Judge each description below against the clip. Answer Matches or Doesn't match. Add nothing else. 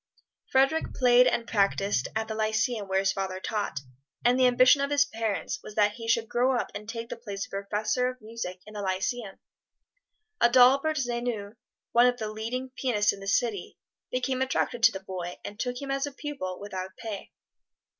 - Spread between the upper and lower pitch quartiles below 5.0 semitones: Matches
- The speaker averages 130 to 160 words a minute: Doesn't match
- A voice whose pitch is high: Matches